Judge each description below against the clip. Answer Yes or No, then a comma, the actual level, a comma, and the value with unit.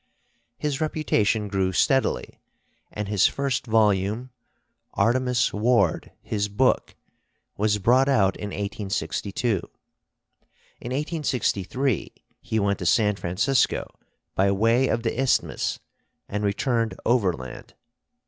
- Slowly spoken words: Yes, slow, 105 wpm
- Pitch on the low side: Yes, low, 110 Hz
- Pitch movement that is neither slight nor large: Yes, average, 4.2 semitones